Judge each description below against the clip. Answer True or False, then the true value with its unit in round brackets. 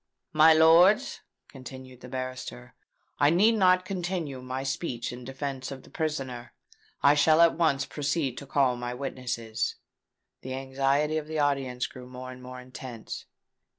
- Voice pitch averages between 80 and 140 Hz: True (135 Hz)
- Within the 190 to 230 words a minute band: False (150 wpm)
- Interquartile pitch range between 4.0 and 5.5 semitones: False (3.6 semitones)